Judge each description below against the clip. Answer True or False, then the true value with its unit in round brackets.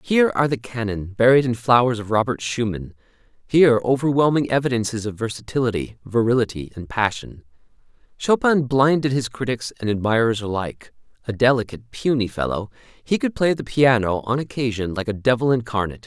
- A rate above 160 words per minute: False (150 wpm)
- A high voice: False (120 Hz)